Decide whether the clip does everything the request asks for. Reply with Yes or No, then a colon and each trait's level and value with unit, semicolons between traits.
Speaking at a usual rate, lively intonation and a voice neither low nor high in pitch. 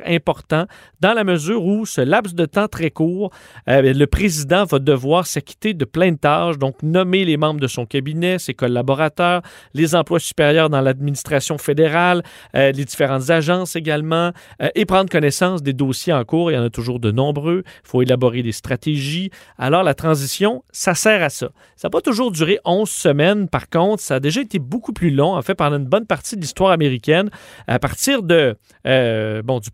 No: average, 200 wpm; average, 5.0 semitones; medium, 160 Hz